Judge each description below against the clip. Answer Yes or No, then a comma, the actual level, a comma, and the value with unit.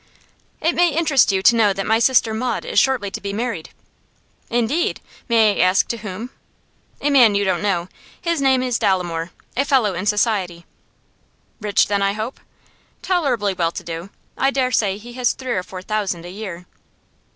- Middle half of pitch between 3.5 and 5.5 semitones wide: Yes, average, 4.8 semitones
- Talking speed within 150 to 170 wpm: No, average, 185 wpm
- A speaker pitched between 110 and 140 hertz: No, high, 215 Hz